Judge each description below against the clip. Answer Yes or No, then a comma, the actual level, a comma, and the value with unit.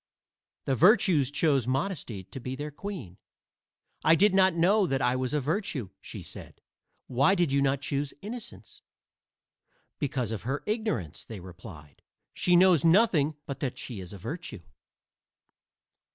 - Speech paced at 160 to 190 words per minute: No, average, 150 wpm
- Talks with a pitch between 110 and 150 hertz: Yes, medium, 140 Hz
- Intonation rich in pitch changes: Yes, wide, 6.5 semitones